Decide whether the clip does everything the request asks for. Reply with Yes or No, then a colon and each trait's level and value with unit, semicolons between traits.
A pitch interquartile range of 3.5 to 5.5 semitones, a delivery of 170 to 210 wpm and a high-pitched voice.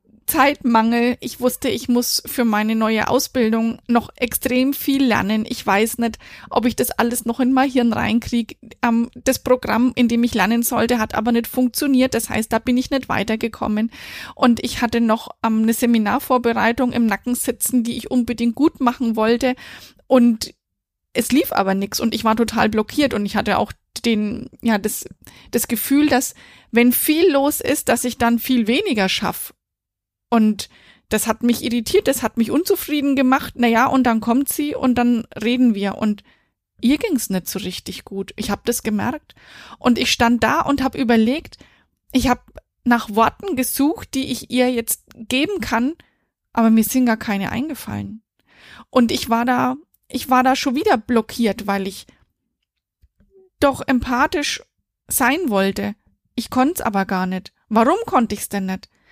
No: narrow, 2.6 semitones; average, 175 wpm; high, 240 Hz